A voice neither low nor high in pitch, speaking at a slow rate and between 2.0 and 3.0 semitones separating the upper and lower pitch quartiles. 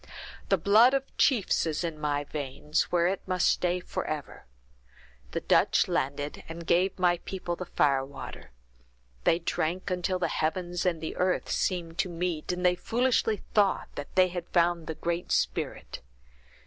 No: medium, 175 Hz; average, 160 wpm; narrow, 2.5 semitones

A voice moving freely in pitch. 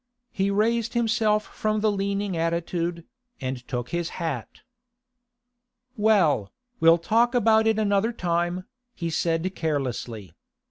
No: average, 4.7 semitones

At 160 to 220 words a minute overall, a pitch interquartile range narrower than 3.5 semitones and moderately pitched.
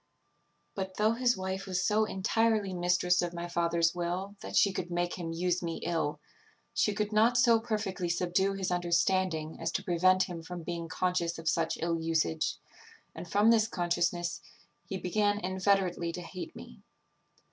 Yes: average, 170 wpm; narrow, 2.4 semitones; medium, 180 Hz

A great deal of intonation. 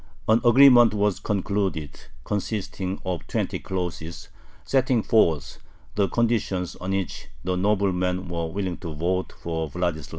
No: average, 3.3 semitones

